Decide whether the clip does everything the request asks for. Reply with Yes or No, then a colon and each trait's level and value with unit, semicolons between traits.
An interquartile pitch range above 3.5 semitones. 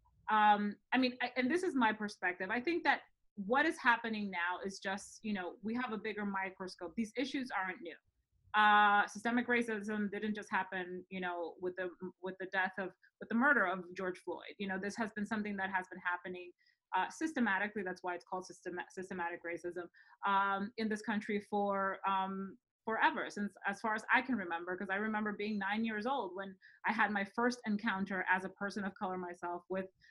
No: average, 2.8 semitones